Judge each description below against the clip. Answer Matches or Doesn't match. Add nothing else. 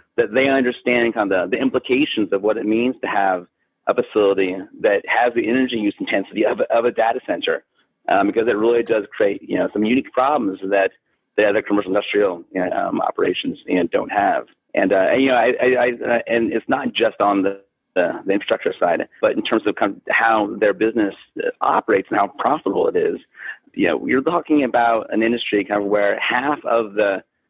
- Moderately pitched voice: Doesn't match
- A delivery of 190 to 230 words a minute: Matches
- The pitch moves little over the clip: Doesn't match